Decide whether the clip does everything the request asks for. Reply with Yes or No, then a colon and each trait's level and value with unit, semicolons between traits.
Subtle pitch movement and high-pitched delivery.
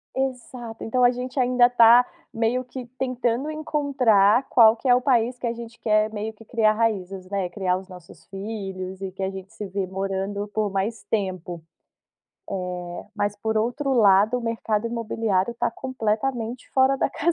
No: average, 3.8 semitones; high, 225 Hz